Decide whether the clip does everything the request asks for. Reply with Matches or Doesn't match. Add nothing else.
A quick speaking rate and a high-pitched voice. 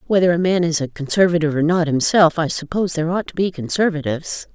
Doesn't match